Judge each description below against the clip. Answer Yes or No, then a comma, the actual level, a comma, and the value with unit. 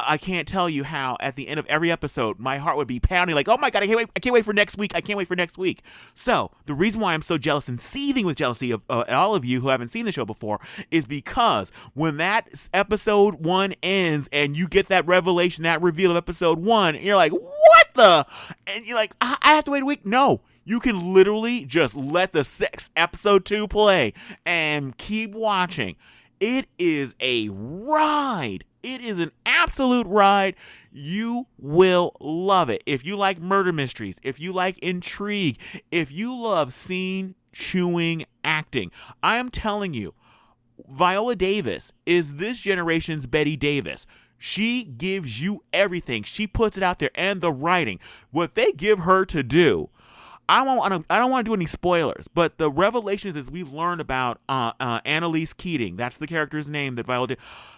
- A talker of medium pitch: Yes, medium, 180 Hz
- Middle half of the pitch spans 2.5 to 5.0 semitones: No, wide, 5.6 semitones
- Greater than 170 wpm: Yes, average, 190 wpm